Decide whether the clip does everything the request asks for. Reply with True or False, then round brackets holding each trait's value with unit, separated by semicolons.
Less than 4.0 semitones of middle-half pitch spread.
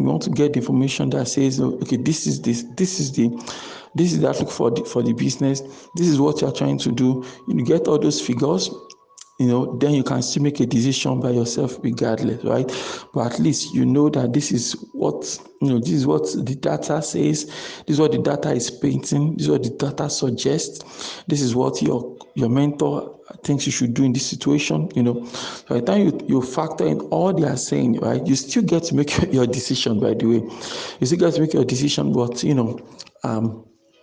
True (3.3 semitones)